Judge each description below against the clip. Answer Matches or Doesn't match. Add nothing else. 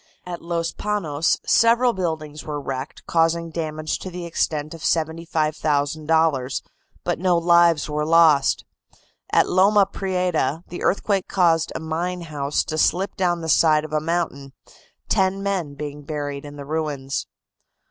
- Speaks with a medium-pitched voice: Matches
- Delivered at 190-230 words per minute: Doesn't match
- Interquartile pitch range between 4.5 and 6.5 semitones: Doesn't match